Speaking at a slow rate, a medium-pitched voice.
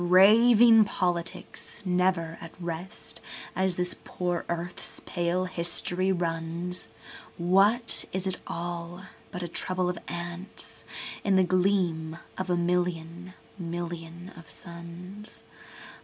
Yes: slow, 105 wpm; medium, 180 Hz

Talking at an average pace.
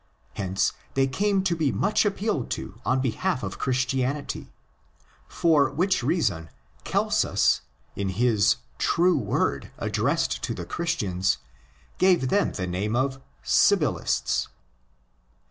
No: slow, 120 wpm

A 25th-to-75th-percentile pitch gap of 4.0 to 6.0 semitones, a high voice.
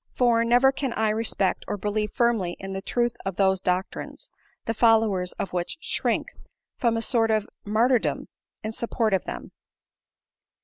No: average, 3.4 semitones; high, 220 Hz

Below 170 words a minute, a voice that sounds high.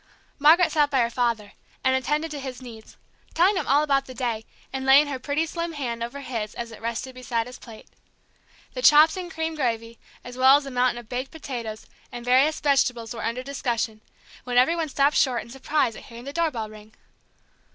No: fast, 205 wpm; very high, 255 Hz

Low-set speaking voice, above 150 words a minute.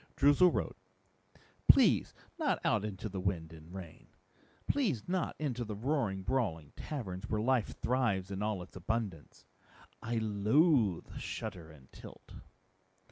No: low, 105 Hz; slow, 135 wpm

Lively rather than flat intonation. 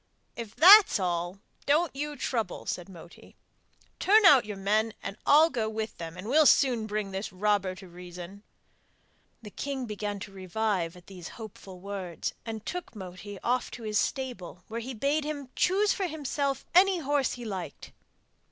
Yes: wide, 6.6 semitones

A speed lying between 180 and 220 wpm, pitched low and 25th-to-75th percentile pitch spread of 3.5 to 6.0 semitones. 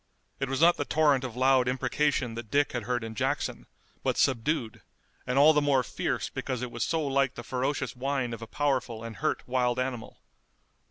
No: average, 200 wpm; low, 130 Hz; average, 2.7 semitones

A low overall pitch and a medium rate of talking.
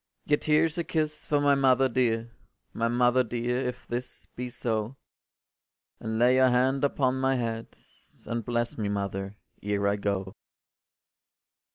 Yes: low, 120 Hz; average, 150 wpm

